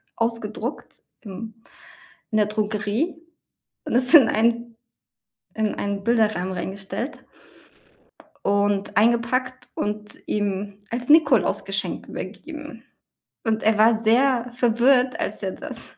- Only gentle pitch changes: No, average, 3.0 semitones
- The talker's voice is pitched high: Yes, high, 225 Hz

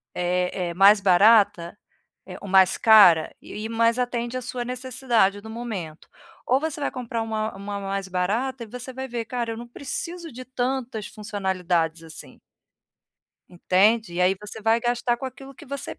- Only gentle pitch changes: No, average, 4.3 semitones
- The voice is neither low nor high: No, high, 225 Hz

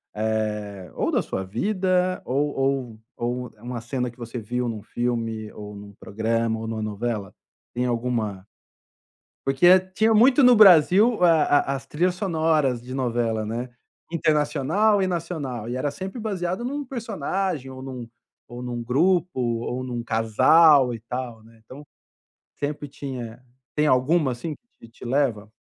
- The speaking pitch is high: No, low, 130 Hz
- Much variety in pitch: Yes, wide, 6.4 semitones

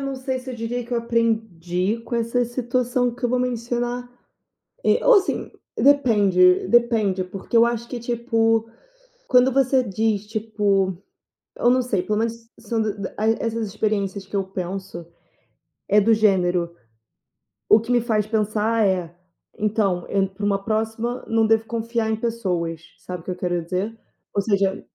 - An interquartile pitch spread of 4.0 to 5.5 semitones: No, average, 3.4 semitones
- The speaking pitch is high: Yes, high, 220 Hz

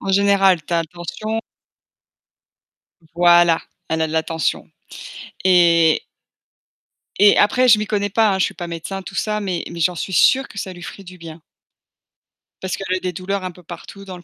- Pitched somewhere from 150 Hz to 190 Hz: Yes, medium, 185 Hz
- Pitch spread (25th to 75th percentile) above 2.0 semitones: Yes, average, 2.8 semitones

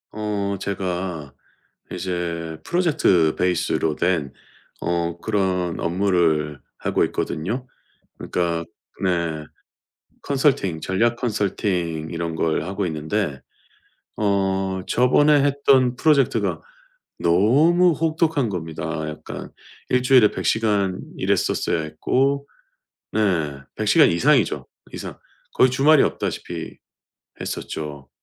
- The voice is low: Yes, very low, 95 Hz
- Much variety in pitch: Yes, wide, 6.8 semitones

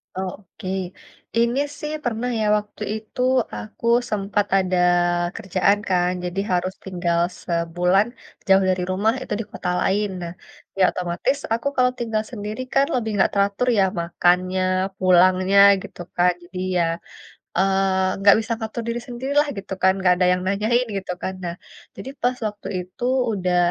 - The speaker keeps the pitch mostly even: No, average, 3.3 semitones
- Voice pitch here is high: Yes, high, 195 Hz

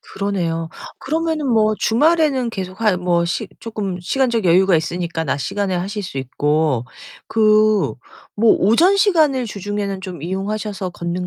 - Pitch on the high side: Yes, high, 200 Hz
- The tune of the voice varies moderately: Yes, average, 4.4 semitones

